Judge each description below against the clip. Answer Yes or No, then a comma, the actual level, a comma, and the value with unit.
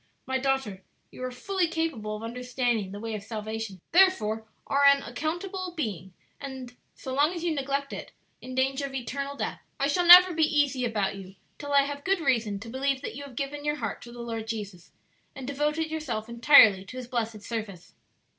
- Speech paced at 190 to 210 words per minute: Yes, average, 200 wpm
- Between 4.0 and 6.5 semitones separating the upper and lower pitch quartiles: Yes, average, 4.5 semitones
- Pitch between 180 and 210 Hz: No, very high, 260 Hz